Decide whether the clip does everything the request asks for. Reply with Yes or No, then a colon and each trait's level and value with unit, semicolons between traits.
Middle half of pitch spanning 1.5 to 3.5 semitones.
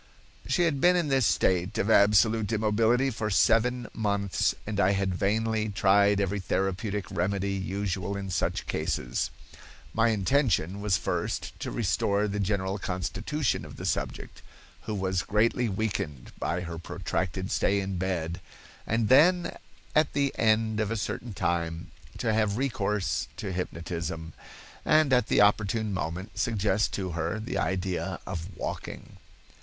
Yes: average, 3.1 semitones